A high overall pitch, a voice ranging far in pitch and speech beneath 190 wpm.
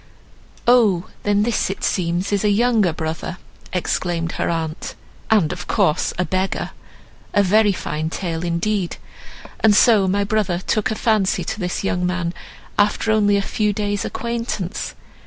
No: high, 195 Hz; average, 3.4 semitones; average, 155 wpm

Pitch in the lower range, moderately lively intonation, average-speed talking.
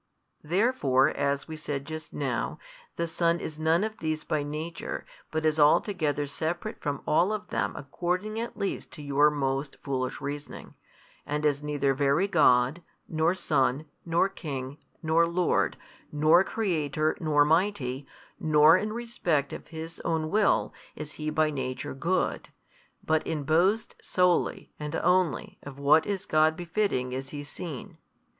No: medium, 155 Hz; average, 3.2 semitones; average, 150 wpm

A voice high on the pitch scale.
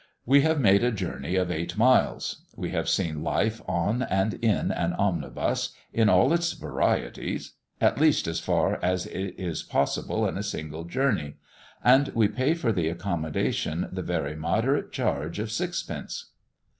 No: low, 100 Hz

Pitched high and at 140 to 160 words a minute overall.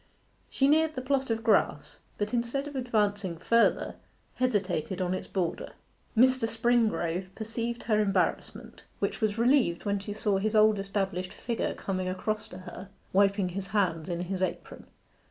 Yes: high, 205 Hz; average, 155 wpm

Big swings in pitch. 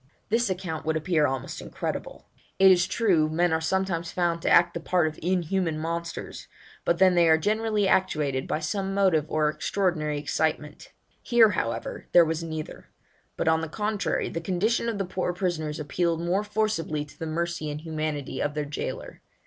No: average, 3.4 semitones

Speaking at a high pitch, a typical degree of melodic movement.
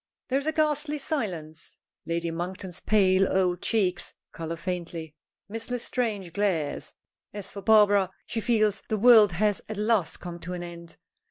Yes: high, 195 Hz; average, 4.1 semitones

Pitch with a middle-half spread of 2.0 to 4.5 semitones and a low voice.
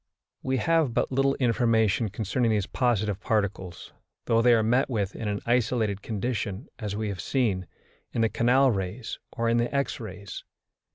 Yes: average, 3.3 semitones; low, 115 Hz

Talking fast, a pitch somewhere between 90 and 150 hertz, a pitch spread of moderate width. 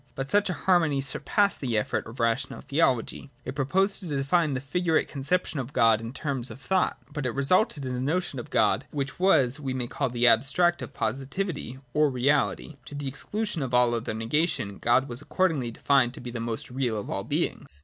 Yes: fast, 210 wpm; low, 135 Hz; average, 4.6 semitones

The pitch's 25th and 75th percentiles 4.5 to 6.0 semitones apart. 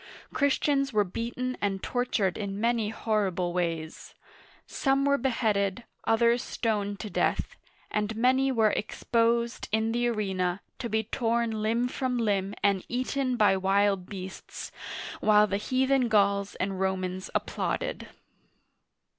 No: average, 3.5 semitones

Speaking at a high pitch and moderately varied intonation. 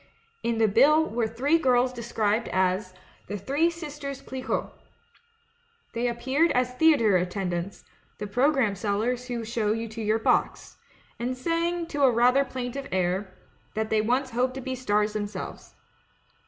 Yes: high, 240 Hz; average, 4.1 semitones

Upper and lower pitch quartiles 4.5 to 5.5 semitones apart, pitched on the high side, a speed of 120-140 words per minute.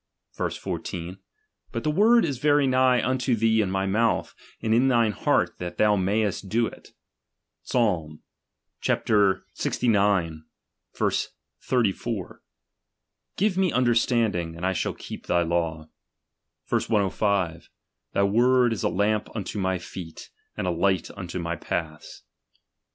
No: average, 4.9 semitones; low, 105 Hz; slow, 135 wpm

